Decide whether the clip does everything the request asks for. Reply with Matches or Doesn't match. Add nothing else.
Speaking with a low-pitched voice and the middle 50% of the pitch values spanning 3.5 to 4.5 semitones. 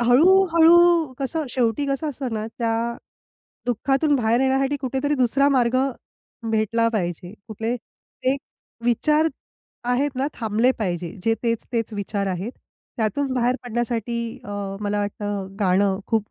Doesn't match